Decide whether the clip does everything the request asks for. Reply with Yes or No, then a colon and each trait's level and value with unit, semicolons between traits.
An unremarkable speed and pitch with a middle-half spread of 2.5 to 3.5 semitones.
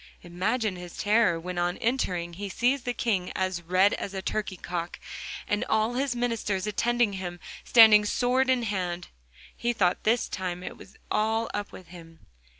No: average, 170 wpm; average, 4.4 semitones